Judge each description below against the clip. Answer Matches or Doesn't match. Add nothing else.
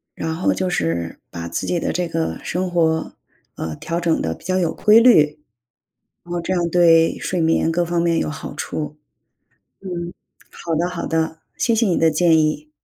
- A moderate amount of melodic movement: Doesn't match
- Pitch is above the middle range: Doesn't match